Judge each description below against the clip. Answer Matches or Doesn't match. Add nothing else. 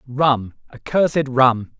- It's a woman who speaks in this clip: Doesn't match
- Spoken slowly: Matches